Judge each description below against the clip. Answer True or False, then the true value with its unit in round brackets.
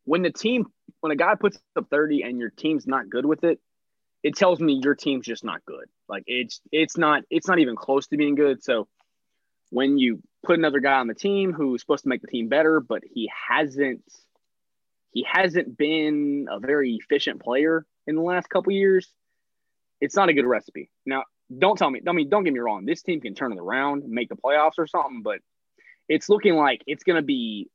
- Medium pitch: True (150 Hz)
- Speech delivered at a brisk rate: True (220 wpm)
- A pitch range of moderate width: True (4.0 semitones)